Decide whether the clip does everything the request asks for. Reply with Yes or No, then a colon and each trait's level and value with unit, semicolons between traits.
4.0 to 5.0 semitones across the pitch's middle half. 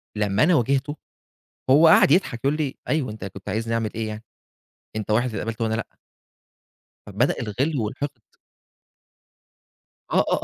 Yes: average, 4.6 semitones